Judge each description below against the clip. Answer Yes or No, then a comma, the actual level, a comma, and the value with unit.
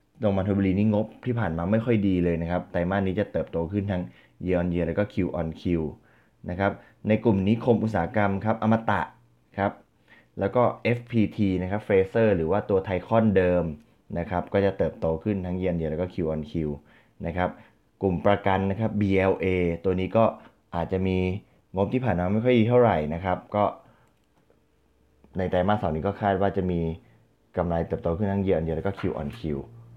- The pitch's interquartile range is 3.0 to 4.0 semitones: Yes, average, 3.6 semitones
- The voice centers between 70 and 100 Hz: Yes, very low, 95 Hz